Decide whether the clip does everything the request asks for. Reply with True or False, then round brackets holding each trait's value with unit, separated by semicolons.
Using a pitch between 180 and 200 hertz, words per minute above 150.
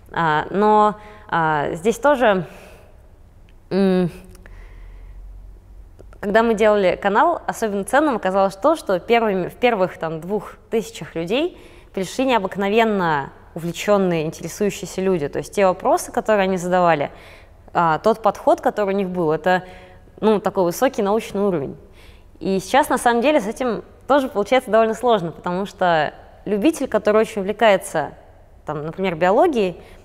False (190 Hz; 130 wpm)